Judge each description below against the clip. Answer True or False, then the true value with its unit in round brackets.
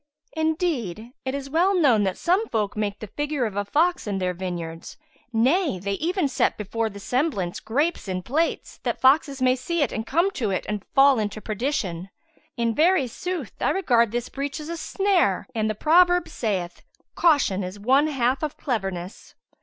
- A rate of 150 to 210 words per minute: True (185 wpm)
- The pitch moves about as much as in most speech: False (7.4 semitones)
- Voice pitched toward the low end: False (250 Hz)